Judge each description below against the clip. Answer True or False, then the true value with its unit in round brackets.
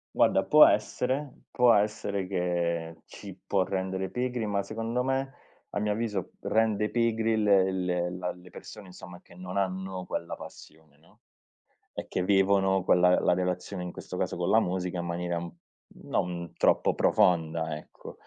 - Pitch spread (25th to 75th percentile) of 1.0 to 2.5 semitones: False (2.9 semitones)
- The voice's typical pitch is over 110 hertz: False (95 Hz)